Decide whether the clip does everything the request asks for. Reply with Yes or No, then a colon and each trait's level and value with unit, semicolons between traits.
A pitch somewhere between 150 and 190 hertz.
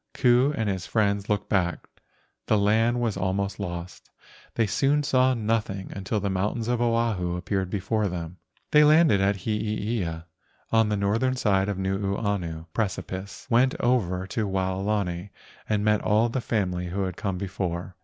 No: low, 100 Hz